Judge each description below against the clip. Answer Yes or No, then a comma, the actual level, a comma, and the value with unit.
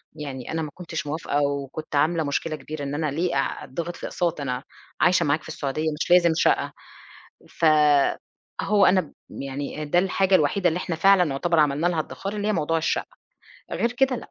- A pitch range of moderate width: Yes, average, 3.7 semitones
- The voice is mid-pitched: Yes, medium, 160 Hz